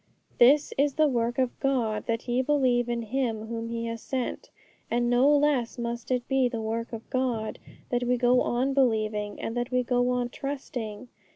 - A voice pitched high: Yes, high, 245 Hz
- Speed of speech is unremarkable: Yes, average, 190 wpm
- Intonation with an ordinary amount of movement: No, narrow, 2.1 semitones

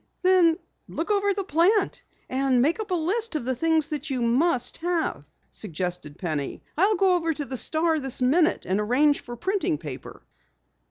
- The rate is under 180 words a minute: Yes, average, 170 wpm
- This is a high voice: Yes, very high, 310 Hz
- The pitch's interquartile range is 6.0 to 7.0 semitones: Yes, wide, 6.7 semitones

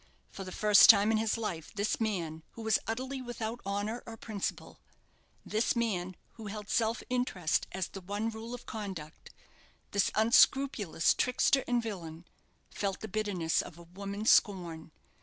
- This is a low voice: No, high, 210 Hz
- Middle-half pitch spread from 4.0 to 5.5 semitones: No, average, 3.3 semitones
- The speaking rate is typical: Yes, average, 160 wpm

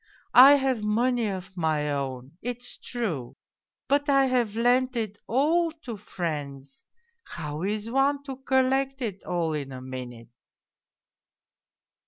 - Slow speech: Yes, slow, 130 wpm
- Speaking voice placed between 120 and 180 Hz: No, high, 215 Hz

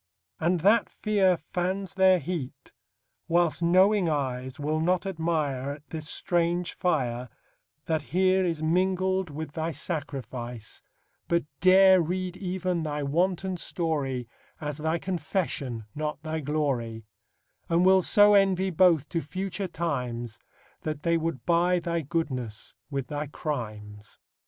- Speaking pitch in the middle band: Yes, medium, 165 Hz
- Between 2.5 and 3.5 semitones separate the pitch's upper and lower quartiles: No, average, 4.3 semitones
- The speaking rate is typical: No, slow, 130 wpm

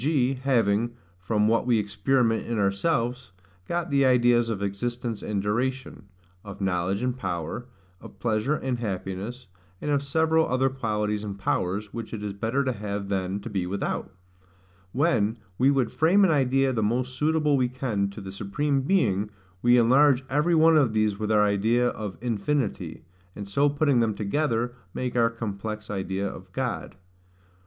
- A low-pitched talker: Yes, low, 115 Hz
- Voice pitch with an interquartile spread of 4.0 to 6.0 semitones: Yes, average, 4.6 semitones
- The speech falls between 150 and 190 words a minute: Yes, average, 165 wpm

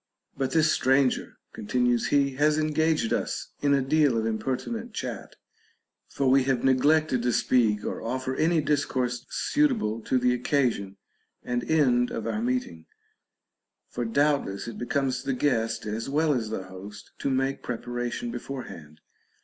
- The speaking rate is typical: Yes, average, 150 wpm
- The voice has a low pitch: Yes, low, 130 Hz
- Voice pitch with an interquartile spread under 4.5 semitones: Yes, average, 3.8 semitones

